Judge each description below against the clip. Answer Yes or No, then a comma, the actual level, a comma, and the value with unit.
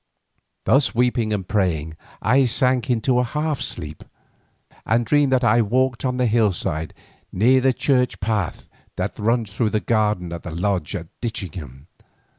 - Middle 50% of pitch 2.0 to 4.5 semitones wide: No, average, 5.0 semitones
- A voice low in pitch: Yes, low, 115 Hz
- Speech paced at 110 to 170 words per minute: Yes, average, 155 wpm